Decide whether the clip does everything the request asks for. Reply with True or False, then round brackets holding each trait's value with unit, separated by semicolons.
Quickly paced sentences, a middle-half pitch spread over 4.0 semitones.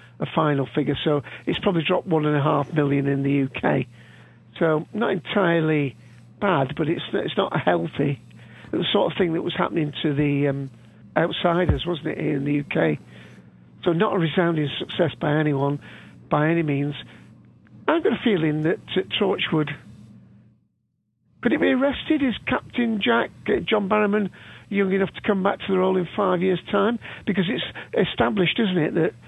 False (180 wpm; 5.2 semitones)